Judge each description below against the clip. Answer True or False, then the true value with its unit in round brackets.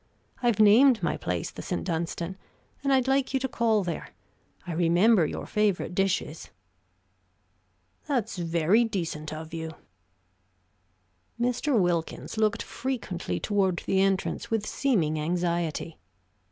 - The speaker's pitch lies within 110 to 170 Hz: False (195 Hz)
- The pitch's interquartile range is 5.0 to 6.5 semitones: True (5.4 semitones)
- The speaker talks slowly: True (125 wpm)